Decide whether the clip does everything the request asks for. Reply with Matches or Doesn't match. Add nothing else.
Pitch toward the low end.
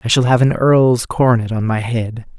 Matches